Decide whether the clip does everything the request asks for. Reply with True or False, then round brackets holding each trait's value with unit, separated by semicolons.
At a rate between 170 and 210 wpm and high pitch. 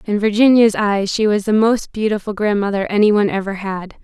True (195 wpm; 205 Hz)